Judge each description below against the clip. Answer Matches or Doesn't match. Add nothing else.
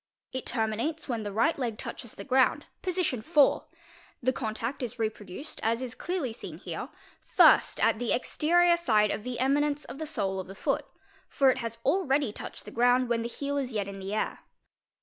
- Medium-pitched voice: Doesn't match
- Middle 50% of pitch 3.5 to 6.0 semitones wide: Matches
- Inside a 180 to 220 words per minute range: Matches